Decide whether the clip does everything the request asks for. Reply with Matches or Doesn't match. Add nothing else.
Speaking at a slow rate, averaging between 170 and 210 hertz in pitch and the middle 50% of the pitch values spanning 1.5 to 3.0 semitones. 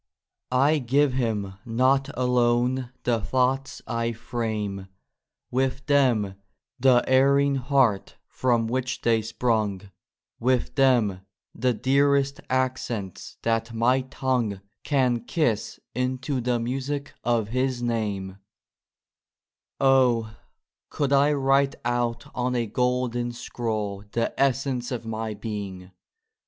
Doesn't match